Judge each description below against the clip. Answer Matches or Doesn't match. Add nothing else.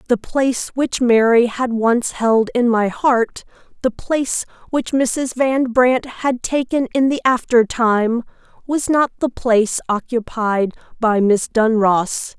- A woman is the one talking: Matches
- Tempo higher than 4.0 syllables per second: Doesn't match